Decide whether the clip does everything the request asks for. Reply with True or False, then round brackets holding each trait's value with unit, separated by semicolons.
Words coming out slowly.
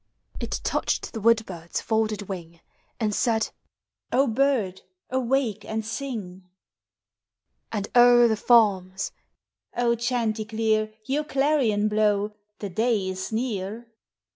True (120 wpm)